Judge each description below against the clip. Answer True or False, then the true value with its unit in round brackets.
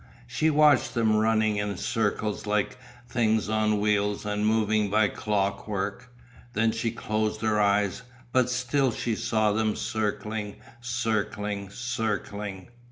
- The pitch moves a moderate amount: False (1.6 semitones)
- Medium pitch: False (110 Hz)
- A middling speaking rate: False (125 wpm)